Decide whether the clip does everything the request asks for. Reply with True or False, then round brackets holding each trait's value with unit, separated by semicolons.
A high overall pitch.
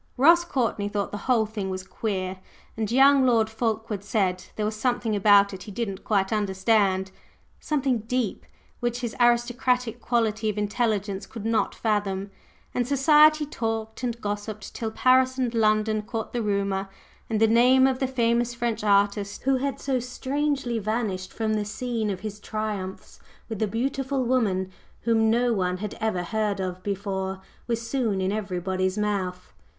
True (220 Hz)